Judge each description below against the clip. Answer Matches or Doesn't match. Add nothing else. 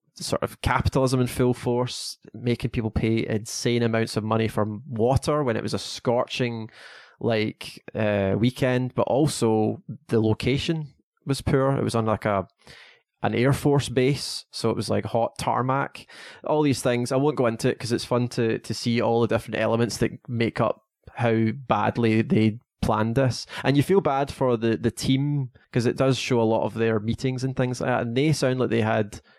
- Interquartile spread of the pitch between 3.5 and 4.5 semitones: Doesn't match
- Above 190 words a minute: Matches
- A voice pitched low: Matches